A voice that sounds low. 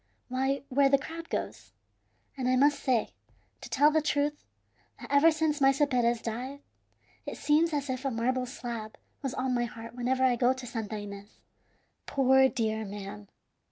No: very high, 260 Hz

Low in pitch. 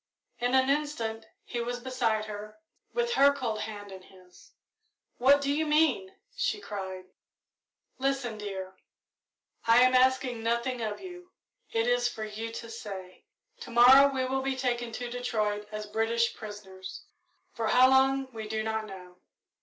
No: high, 235 Hz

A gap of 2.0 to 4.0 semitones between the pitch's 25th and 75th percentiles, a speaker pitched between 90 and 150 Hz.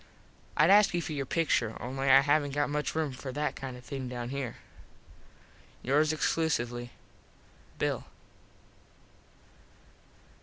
Yes: average, 3.2 semitones; medium, 140 Hz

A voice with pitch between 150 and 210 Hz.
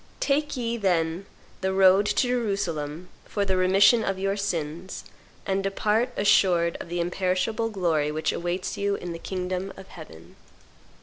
Yes: high, 190 Hz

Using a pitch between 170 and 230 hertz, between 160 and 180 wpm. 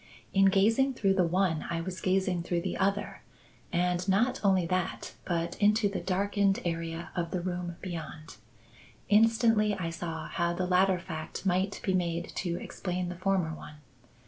Yes: medium, 185 Hz; average, 165 wpm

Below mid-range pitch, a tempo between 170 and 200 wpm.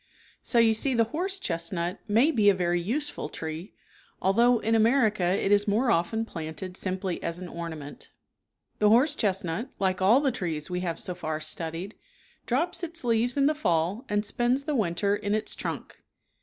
No: high, 205 Hz; average, 185 wpm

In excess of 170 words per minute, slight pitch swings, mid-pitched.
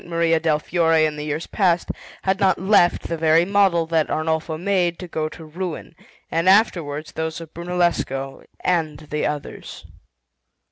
No: average, 160 wpm; narrow, 2.3 semitones; medium, 165 Hz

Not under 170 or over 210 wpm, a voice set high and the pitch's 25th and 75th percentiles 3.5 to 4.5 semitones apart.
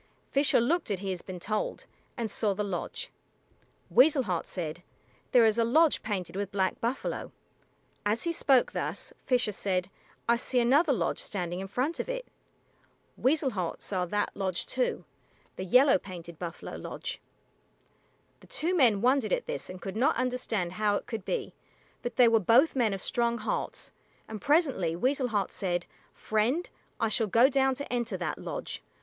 No: average, 175 wpm; high, 225 Hz; wide, 5.4 semitones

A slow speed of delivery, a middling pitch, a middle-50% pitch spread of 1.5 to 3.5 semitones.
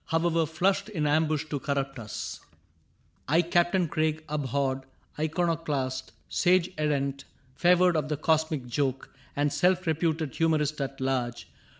Yes: slow, 130 wpm; medium, 155 Hz; average, 3.2 semitones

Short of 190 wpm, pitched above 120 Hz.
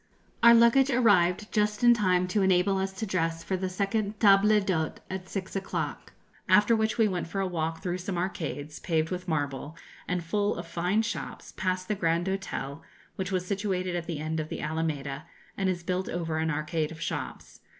No: average, 200 wpm; medium, 185 Hz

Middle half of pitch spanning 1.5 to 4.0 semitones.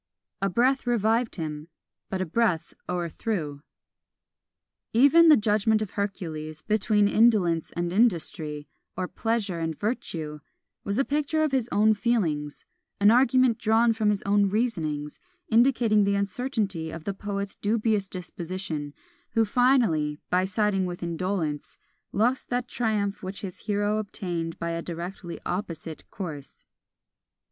No: average, 5.0 semitones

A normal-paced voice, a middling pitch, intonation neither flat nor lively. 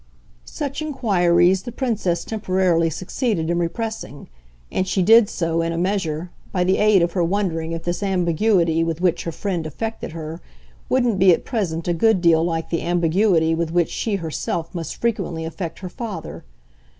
Yes: average, 175 wpm; medium, 175 Hz; average, 3.5 semitones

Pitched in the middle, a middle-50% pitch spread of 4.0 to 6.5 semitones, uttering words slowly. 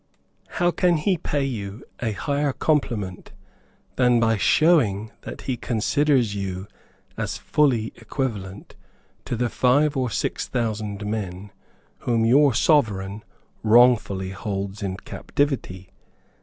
No: low, 115 Hz; average, 5.3 semitones; slow, 115 wpm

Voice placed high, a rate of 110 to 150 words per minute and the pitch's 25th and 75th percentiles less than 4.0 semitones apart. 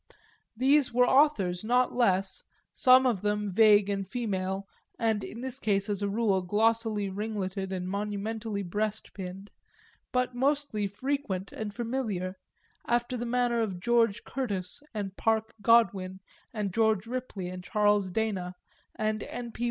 Yes: high, 210 Hz; average, 140 wpm; average, 3.4 semitones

